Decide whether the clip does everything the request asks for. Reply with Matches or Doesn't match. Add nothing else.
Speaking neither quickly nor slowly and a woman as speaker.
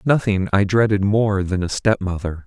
Doesn't match